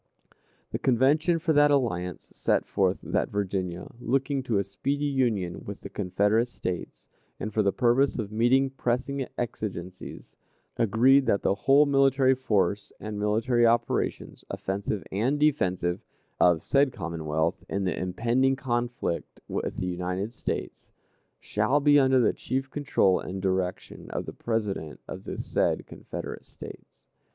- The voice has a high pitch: No, low, 115 Hz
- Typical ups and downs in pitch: No, wide, 5.8 semitones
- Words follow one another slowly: No, average, 145 wpm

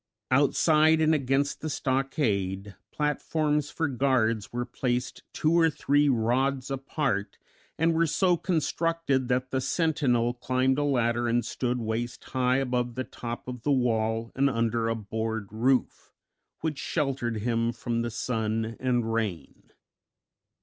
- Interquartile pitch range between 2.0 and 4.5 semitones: Yes, average, 3.7 semitones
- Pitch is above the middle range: No, low, 125 Hz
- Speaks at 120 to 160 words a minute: Yes, average, 140 wpm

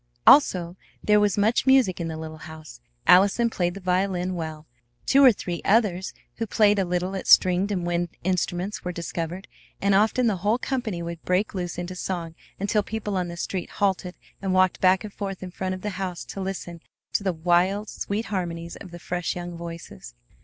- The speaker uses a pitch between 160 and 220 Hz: Yes, medium, 185 Hz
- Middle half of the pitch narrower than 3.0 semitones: Yes, narrow, 2.6 semitones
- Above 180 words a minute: Yes, average, 195 wpm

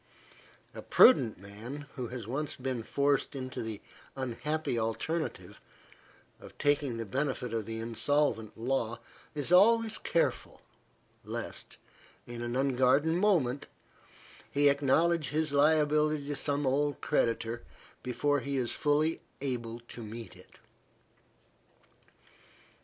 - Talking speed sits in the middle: No, slow, 115 wpm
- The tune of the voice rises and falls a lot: No, average, 3.9 semitones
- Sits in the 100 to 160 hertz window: Yes, low, 135 Hz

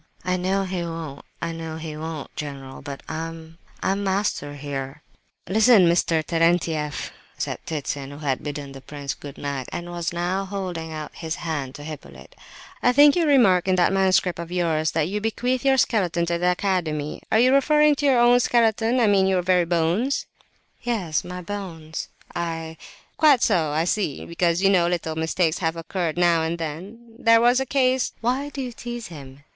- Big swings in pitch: No, average, 4.7 semitones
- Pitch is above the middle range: No, medium, 175 Hz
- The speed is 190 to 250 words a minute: No, average, 180 wpm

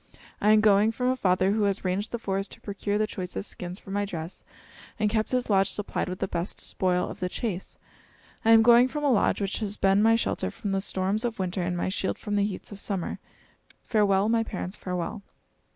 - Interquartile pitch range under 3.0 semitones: Yes, narrow, 2.5 semitones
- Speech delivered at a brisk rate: Yes, fast, 225 wpm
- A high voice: Yes, high, 200 Hz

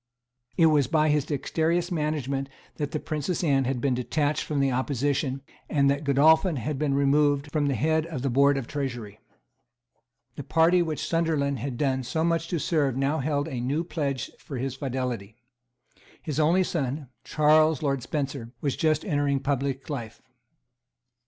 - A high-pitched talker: No, medium, 145 Hz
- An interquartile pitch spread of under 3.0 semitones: Yes, narrow, 2.5 semitones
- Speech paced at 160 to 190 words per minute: Yes, average, 170 wpm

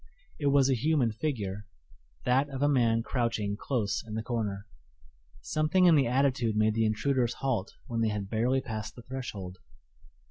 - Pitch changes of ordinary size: Yes, average, 3.8 semitones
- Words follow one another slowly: No, average, 170 wpm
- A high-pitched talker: No, low, 120 Hz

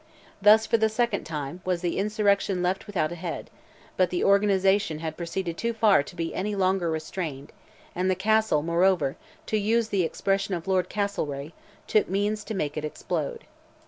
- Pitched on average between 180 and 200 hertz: Yes, high, 190 Hz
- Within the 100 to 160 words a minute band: No, average, 175 wpm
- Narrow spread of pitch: No, average, 3.7 semitones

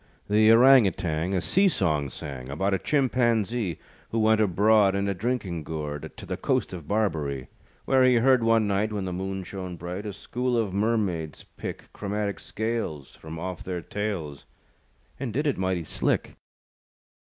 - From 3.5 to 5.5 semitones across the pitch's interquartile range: Yes, average, 4.6 semitones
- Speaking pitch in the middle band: No, low, 100 Hz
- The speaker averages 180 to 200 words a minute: No, average, 165 wpm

